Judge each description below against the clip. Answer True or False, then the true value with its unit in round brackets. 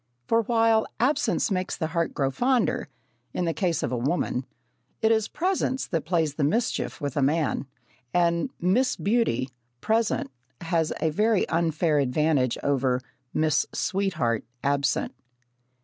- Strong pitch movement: True (7.5 semitones)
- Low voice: False (165 Hz)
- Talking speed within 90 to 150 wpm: True (140 wpm)